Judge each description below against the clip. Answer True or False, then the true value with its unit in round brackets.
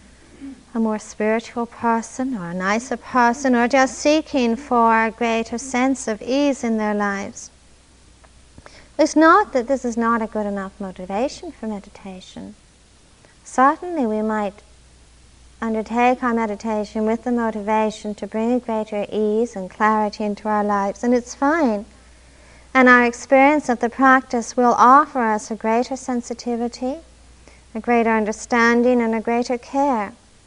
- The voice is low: False (235 Hz)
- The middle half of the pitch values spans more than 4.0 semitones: False (2.8 semitones)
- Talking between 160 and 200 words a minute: False (145 wpm)